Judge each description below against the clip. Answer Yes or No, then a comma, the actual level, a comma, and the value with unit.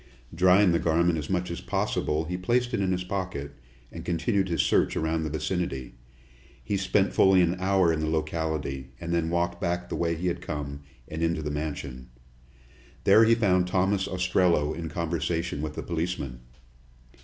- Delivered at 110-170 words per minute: No, average, 180 wpm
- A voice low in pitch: Yes, very low, 85 Hz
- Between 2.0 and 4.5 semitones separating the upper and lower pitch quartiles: Yes, average, 2.8 semitones